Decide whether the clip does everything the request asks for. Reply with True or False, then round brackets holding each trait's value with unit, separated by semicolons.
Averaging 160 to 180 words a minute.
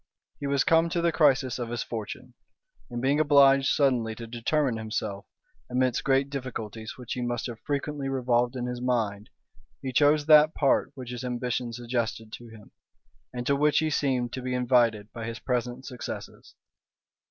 True (175 wpm)